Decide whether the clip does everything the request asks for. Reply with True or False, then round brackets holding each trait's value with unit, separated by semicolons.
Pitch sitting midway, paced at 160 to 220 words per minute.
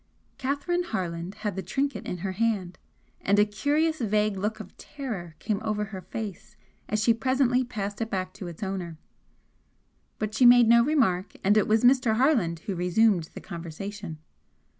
False (210 Hz; 170 wpm)